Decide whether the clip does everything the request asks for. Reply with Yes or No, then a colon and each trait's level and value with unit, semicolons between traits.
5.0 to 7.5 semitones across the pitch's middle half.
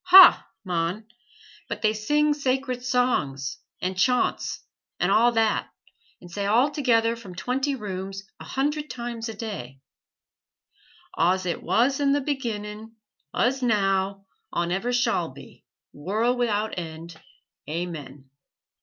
Yes: average, 5.3 semitones